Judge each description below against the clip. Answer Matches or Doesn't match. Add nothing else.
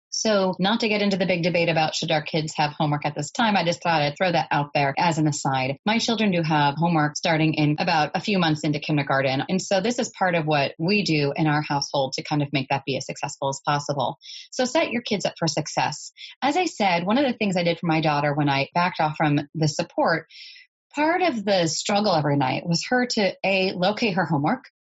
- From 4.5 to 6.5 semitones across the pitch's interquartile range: Matches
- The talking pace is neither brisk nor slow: Doesn't match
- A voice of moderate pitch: Matches